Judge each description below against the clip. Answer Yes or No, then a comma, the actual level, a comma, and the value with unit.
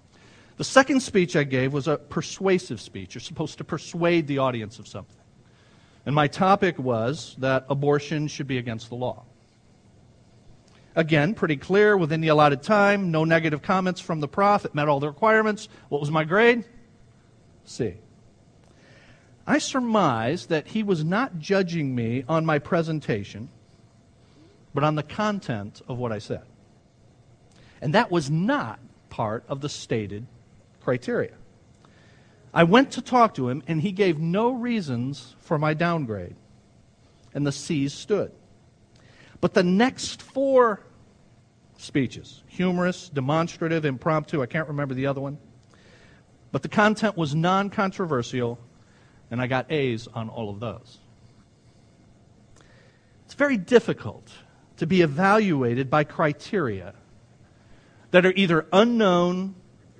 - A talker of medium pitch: Yes, medium, 145 Hz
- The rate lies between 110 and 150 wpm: Yes, slow, 135 wpm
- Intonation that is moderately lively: No, wide, 7.1 semitones